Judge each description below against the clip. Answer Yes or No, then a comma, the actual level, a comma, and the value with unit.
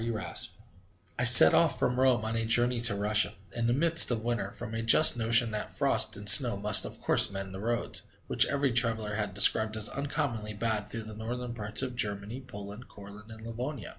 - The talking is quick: Yes, fast, 210 wpm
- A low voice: Yes, low, 115 Hz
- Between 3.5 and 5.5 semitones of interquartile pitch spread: No, narrow, 2.6 semitones